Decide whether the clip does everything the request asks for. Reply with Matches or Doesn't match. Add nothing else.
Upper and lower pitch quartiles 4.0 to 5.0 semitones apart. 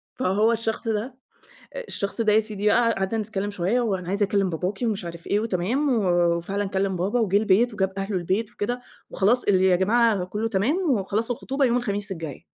Doesn't match